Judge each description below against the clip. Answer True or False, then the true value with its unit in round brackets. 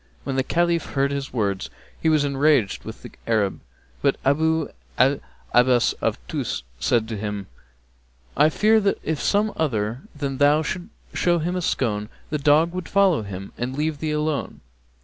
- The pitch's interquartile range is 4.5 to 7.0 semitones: True (4.9 semitones)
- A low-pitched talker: False (145 Hz)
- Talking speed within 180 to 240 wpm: False (170 wpm)